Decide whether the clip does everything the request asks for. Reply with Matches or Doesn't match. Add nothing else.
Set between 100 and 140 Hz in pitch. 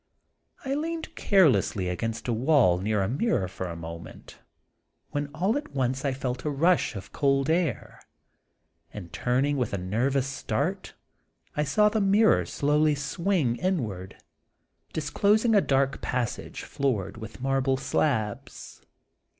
Matches